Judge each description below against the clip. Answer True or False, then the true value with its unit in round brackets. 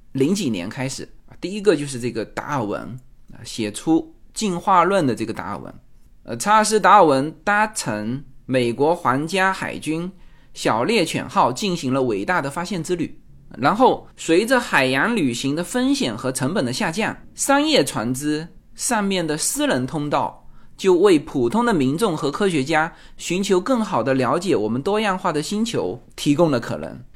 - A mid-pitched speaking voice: True (165 Hz)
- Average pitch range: False (7.8 semitones)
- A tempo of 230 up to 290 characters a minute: True (255 characters per minute)